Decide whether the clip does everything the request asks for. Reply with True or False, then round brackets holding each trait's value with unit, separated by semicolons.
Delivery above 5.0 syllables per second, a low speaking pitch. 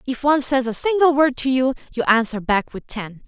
False (5.5 syllables/s; 255 Hz)